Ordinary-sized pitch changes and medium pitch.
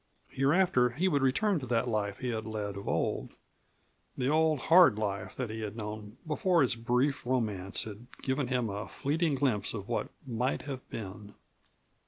No: average, 4.7 semitones; low, 125 Hz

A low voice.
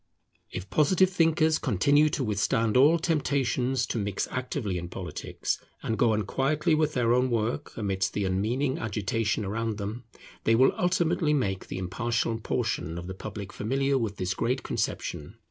Yes: low, 120 Hz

